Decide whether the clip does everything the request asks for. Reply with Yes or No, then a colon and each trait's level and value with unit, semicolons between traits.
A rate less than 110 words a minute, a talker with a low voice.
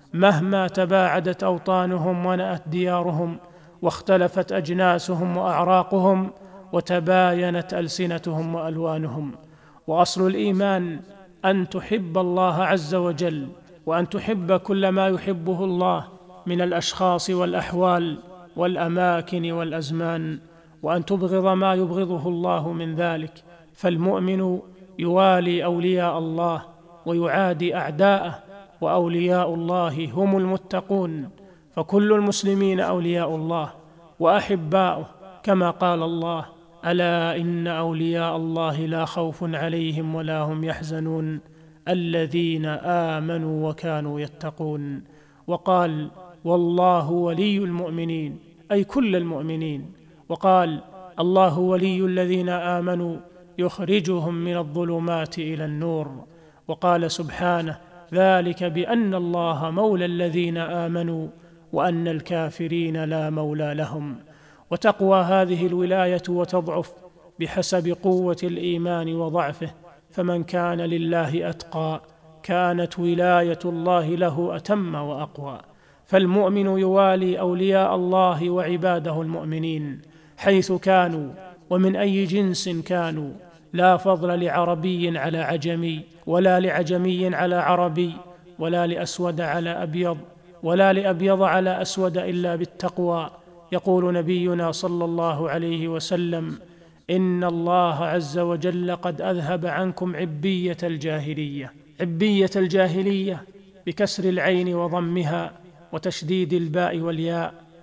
No: average, 95 wpm; medium, 175 Hz